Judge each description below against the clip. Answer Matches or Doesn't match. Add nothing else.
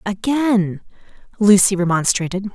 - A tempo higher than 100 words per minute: Doesn't match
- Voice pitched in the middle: Doesn't match